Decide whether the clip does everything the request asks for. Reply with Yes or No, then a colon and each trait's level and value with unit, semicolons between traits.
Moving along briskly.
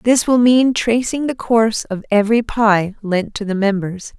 No: average, 185 wpm